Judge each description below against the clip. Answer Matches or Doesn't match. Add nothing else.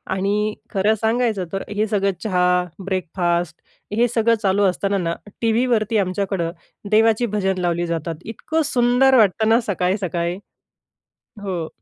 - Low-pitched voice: Doesn't match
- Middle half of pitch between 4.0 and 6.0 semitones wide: Doesn't match